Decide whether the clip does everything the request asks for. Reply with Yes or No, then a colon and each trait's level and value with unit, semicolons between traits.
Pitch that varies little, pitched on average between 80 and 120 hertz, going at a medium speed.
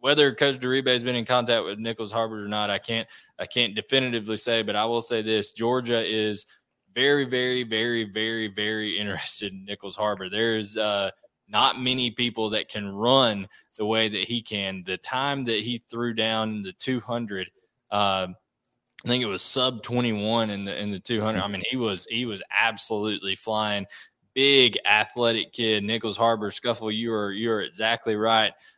Yes: narrow, 2.3 semitones; low, 110 Hz; average, 185 wpm